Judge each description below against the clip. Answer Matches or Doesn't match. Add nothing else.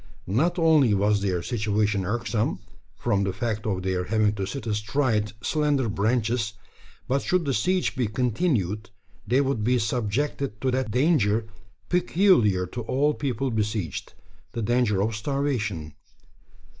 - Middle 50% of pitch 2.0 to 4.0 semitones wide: Doesn't match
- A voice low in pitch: Matches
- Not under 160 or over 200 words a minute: Doesn't match